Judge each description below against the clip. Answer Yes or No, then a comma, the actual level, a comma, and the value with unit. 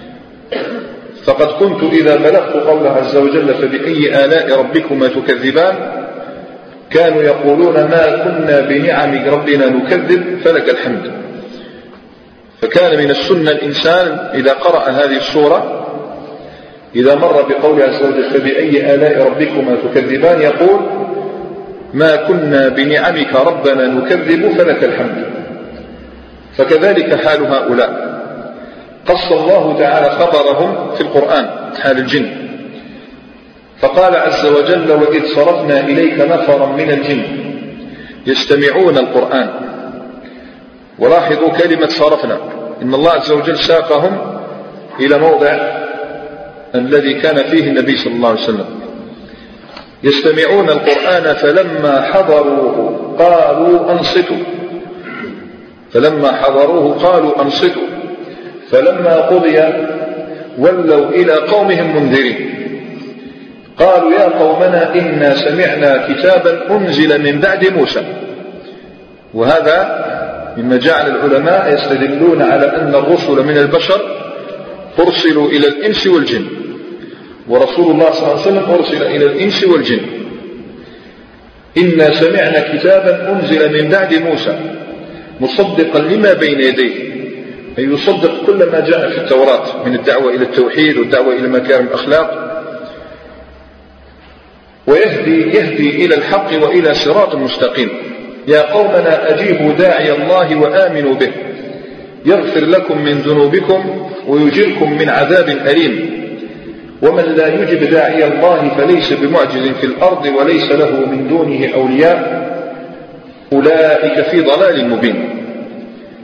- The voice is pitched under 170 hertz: Yes, medium, 155 Hz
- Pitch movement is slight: No, average, 4.4 semitones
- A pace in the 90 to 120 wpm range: Yes, average, 105 wpm